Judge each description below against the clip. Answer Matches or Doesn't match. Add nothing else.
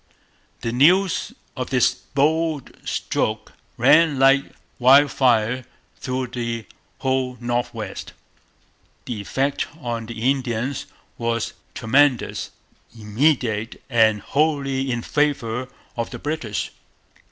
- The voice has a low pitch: Matches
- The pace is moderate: Doesn't match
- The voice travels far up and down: Doesn't match